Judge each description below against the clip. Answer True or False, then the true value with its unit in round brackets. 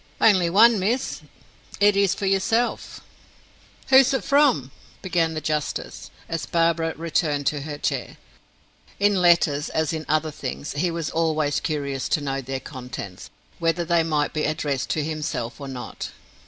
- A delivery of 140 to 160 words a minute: True (155 wpm)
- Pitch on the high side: False (160 Hz)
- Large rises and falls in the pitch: False (3.7 semitones)